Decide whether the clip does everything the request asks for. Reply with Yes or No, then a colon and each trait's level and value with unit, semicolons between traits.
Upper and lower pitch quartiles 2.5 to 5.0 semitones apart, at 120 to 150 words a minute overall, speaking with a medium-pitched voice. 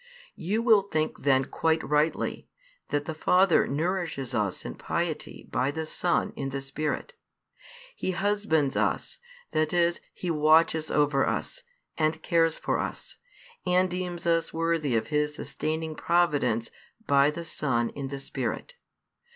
Yes: average, 3.3 semitones; average, 145 wpm; medium, 160 Hz